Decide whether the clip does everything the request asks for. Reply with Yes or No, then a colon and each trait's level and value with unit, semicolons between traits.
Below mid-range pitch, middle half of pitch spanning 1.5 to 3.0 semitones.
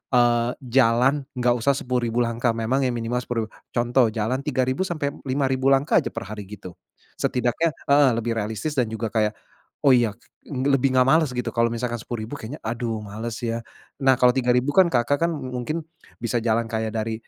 Yes: low, 120 Hz; narrow, 2.6 semitones